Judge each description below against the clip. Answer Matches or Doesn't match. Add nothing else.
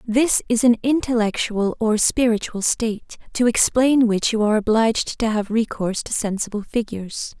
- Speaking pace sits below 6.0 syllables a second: Matches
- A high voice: Matches